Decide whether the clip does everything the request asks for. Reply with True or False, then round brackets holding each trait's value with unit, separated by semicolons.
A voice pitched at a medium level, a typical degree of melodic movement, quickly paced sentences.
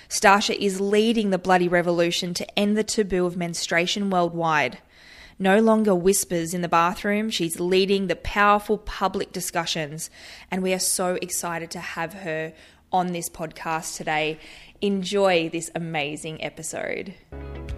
False (180 Hz; 3.0 semitones; 140 wpm)